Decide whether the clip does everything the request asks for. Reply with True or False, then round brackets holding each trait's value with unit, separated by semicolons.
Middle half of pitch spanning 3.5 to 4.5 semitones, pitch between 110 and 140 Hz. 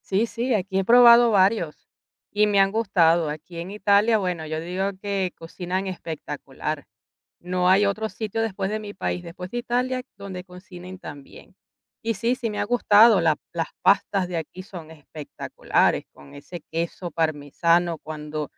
False (4.0 semitones; 185 Hz)